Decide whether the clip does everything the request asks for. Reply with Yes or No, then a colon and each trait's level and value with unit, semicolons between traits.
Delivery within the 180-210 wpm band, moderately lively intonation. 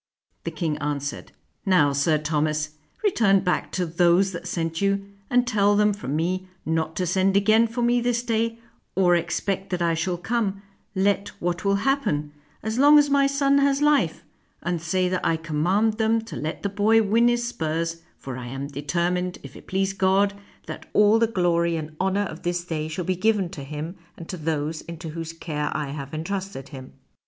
Yes: average, 200 wpm; average, 4.5 semitones